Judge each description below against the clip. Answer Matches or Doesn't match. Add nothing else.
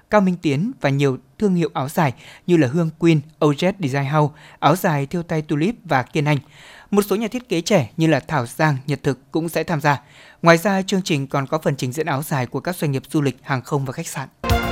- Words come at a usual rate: Doesn't match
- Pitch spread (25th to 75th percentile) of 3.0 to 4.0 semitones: Matches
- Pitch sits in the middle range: Matches